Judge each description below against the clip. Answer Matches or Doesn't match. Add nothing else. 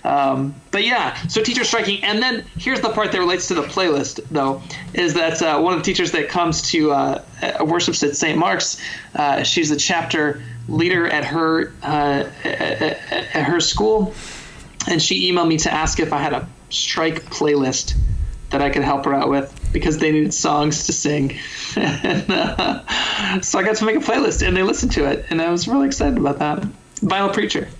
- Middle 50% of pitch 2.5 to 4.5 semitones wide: Doesn't match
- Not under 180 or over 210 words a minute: Matches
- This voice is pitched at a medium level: Matches